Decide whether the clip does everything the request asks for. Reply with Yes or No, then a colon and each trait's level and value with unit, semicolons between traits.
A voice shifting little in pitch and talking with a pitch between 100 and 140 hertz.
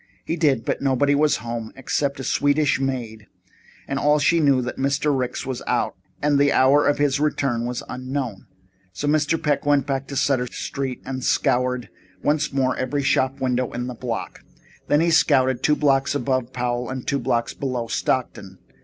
Yes: narrow, 2.3 semitones; low, 135 Hz